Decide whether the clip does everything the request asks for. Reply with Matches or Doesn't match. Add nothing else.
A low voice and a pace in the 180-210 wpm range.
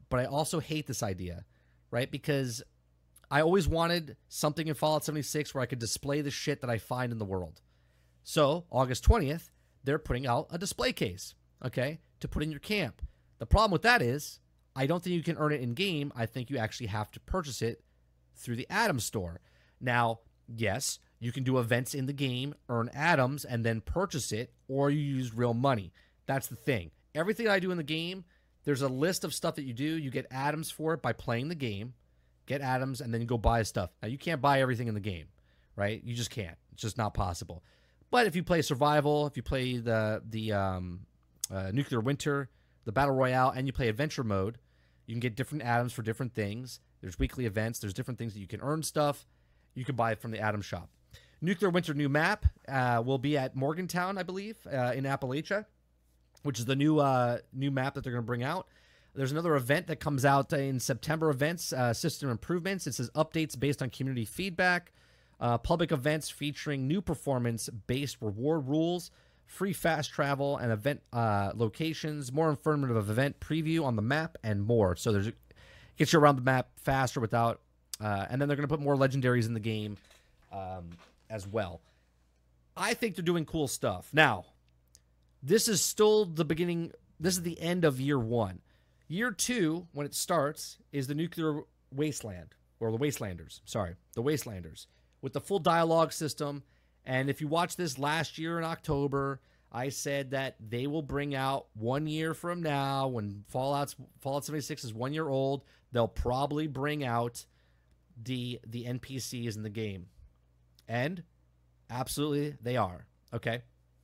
Matches